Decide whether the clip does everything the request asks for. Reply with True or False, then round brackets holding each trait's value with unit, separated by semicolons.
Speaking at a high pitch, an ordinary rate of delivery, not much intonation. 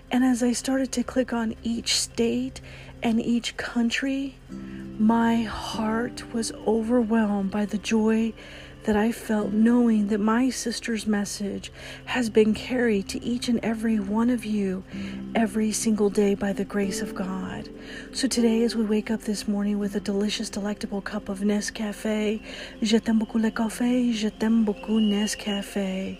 True (220 Hz; 160 wpm; 2.0 semitones)